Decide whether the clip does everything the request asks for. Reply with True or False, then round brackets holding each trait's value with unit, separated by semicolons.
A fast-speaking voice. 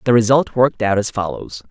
True (210 wpm)